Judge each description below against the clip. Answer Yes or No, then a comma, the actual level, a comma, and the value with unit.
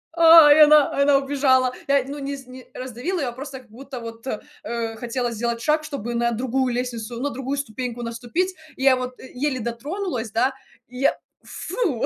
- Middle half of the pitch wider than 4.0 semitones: No, average, 3.0 semitones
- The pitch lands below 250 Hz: No, very high, 255 Hz